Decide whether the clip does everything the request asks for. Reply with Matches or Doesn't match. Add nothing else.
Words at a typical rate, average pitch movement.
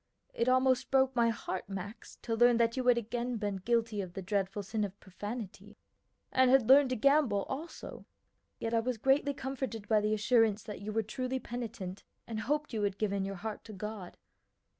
Matches